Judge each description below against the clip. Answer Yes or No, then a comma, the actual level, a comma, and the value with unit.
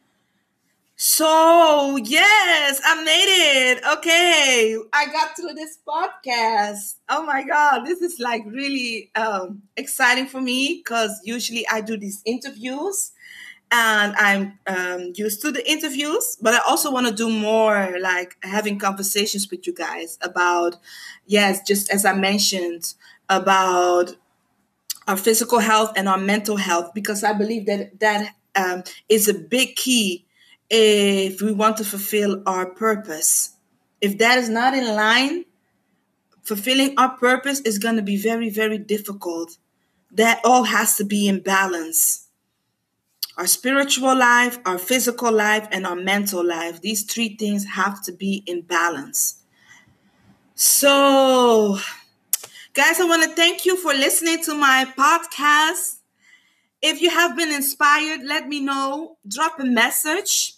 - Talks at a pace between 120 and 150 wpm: Yes, average, 140 wpm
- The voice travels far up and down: Yes, wide, 5.9 semitones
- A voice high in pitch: Yes, high, 225 Hz